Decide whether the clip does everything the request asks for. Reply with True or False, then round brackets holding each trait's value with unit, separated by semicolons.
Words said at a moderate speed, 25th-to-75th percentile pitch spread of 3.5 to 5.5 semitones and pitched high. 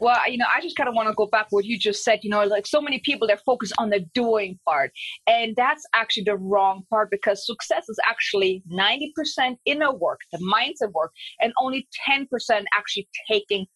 False (210 wpm; 4.6 semitones; 220 Hz)